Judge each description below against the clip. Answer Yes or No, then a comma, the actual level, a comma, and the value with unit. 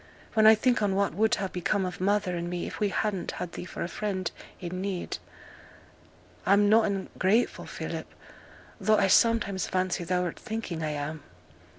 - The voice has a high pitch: Yes, high, 195 Hz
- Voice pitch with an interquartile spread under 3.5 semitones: Yes, average, 2.8 semitones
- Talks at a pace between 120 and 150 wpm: No, average, 175 wpm